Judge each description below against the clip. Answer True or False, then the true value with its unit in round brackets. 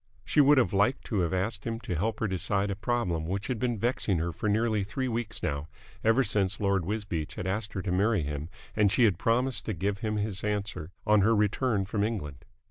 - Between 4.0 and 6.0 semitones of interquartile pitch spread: False (3.1 semitones)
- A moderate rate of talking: False (220 wpm)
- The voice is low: True (105 Hz)